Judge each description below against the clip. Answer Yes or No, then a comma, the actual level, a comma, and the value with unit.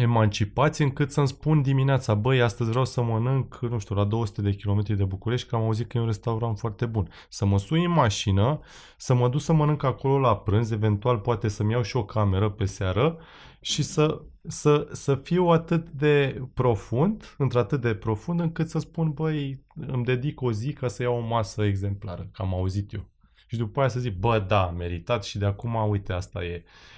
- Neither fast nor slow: No, fast, 205 wpm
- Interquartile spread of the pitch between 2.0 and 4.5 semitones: No, average, 5.1 semitones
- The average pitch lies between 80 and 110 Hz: No, low, 120 Hz